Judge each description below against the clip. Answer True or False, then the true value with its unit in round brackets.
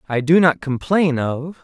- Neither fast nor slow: True (185 wpm)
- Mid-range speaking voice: True (150 Hz)